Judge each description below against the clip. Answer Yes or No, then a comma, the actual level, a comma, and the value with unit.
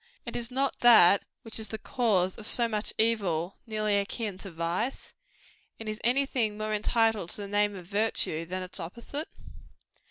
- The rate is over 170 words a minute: Yes, average, 180 wpm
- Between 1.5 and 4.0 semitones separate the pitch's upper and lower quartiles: Yes, average, 3.3 semitones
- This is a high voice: Yes, high, 215 Hz